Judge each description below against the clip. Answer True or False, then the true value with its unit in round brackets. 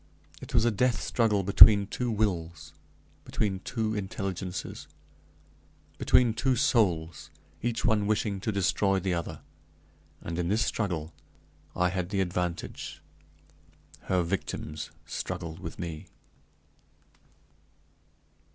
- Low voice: True (95 Hz)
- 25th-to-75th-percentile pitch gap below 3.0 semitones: False (3.9 semitones)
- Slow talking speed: True (110 wpm)